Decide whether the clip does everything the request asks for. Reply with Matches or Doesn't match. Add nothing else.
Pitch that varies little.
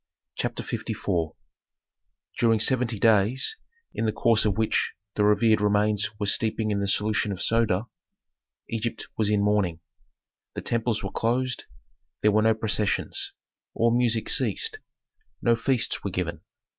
Matches